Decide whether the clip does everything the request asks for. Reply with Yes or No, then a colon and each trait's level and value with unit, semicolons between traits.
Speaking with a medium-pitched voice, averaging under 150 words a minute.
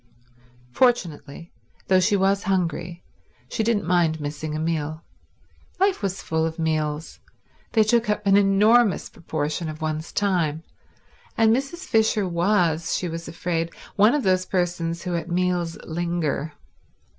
Yes: medium, 175 Hz; average, 140 wpm